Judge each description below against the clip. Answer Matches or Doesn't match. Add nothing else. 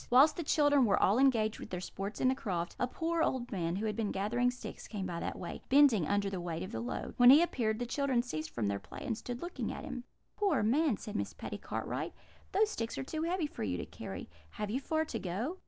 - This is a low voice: Doesn't match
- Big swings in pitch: Matches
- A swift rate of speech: Matches